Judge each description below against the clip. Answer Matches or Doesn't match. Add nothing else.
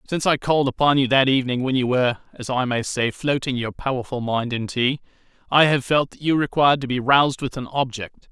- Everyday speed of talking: Doesn't match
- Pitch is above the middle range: Doesn't match